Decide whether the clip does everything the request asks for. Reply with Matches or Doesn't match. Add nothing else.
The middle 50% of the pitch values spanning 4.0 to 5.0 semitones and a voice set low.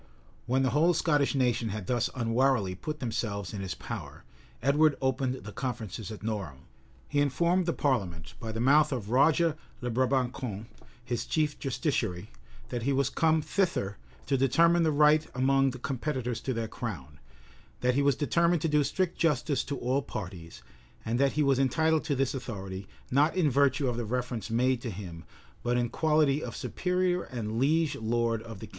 Matches